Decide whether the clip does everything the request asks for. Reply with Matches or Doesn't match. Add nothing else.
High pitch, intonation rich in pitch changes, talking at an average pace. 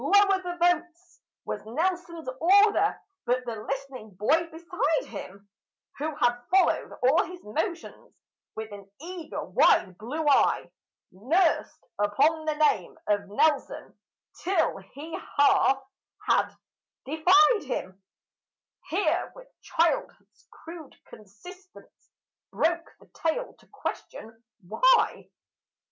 Doesn't match